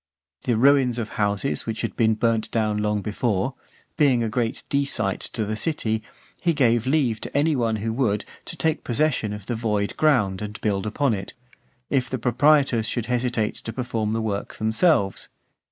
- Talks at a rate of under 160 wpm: No, average, 180 wpm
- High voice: No, low, 115 Hz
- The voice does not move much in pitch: No, average, 3.4 semitones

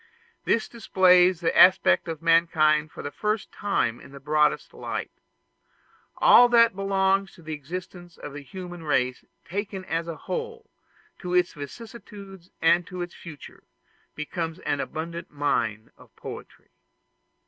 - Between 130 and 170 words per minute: Yes, average, 140 wpm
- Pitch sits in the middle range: Yes, medium, 175 Hz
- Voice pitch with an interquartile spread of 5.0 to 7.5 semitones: No, average, 4.0 semitones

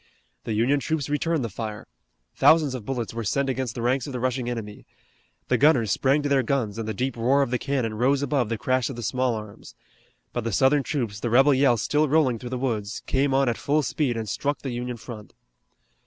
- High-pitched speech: No, low, 125 Hz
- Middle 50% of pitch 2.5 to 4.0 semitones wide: Yes, average, 3.3 semitones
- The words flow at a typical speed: No, fast, 230 wpm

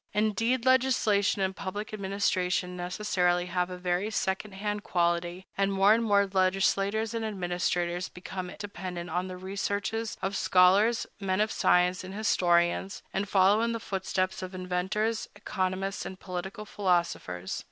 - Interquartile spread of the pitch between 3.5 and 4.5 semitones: No, narrow, 2.5 semitones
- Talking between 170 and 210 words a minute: No, average, 140 wpm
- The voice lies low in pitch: No, high, 190 Hz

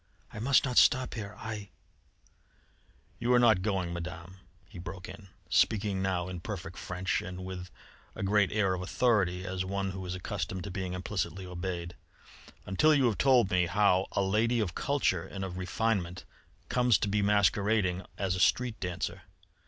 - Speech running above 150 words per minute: Yes, average, 175 wpm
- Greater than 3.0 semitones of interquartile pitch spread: No, narrow, 2.6 semitones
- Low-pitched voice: Yes, very low, 95 Hz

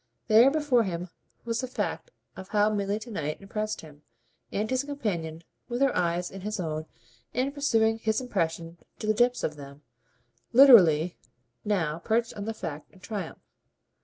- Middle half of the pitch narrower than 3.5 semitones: No, wide, 5.6 semitones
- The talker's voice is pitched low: No, high, 210 Hz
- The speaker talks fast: No, average, 165 wpm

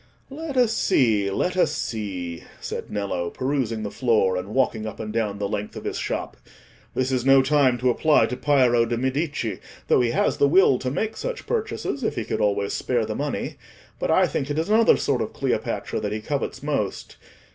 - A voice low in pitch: Yes, low, 125 Hz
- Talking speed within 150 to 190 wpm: No, fast, 205 wpm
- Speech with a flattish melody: No, wide, 5.4 semitones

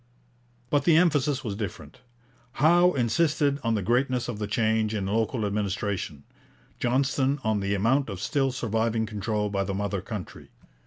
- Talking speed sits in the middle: Yes, average, 155 wpm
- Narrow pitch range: No, average, 4.7 semitones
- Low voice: Yes, low, 110 Hz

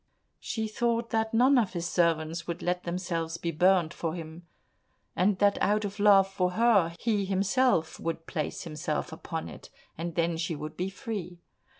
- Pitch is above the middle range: No, medium, 180 Hz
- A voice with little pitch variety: No, average, 3.6 semitones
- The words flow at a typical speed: Yes, average, 175 wpm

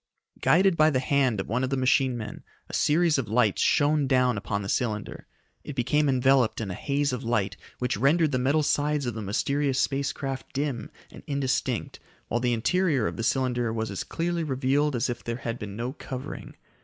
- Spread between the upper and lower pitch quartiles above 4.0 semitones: No, average, 3.6 semitones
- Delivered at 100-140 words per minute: No, fast, 205 wpm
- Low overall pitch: Yes, low, 130 Hz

